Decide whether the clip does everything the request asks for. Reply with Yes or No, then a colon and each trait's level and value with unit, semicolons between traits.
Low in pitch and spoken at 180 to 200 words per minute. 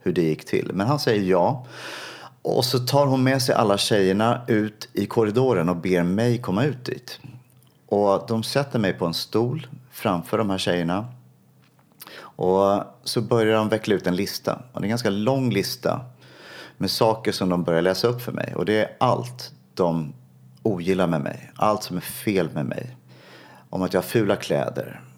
Yes: low, 105 Hz; average, 190 wpm